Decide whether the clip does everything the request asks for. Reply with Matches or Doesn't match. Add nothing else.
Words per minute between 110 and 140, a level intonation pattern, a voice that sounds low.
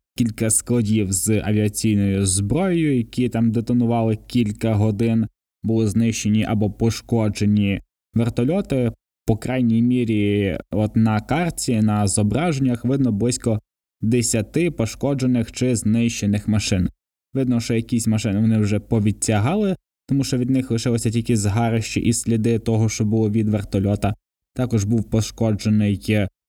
Matches